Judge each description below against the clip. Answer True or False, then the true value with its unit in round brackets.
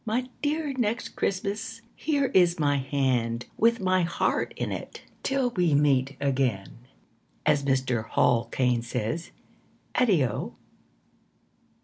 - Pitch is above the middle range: False (150 Hz)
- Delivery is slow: True (115 wpm)